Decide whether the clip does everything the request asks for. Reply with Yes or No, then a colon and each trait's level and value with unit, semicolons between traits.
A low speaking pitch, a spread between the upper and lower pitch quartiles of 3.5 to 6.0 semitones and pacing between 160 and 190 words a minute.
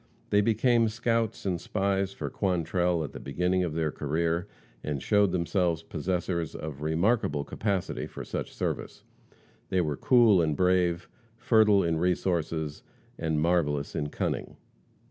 No: very low, 90 Hz; average, 3.9 semitones; average, 140 wpm